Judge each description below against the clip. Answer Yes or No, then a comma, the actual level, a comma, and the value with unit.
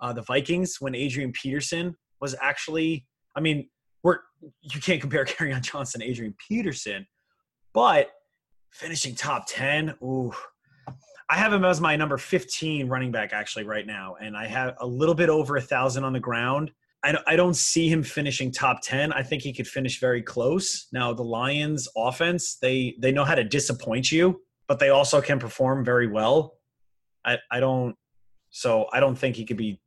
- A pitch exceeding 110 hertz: Yes, low, 135 Hz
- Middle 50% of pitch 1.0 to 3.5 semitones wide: No, average, 4.2 semitones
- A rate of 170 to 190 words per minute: Yes, average, 180 wpm